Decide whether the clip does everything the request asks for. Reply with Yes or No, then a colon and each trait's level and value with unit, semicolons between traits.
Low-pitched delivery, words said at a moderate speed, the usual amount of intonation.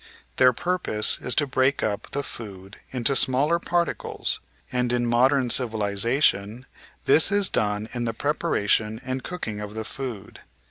Yes: low, 125 Hz; average, 150 wpm; average, 4.4 semitones